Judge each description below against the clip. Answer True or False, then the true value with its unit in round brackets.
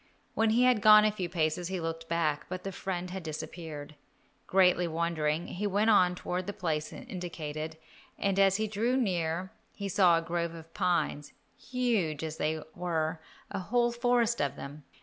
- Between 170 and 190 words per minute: True (175 wpm)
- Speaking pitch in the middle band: True (175 Hz)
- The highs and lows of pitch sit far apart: False (3.9 semitones)